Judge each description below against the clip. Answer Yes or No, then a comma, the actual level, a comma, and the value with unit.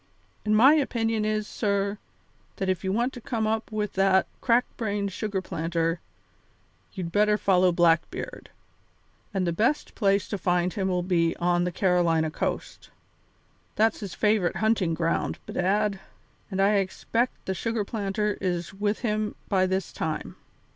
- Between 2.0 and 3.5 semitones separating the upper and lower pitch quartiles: Yes, average, 3.1 semitones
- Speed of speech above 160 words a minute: No, average, 155 wpm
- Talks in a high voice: Yes, high, 195 Hz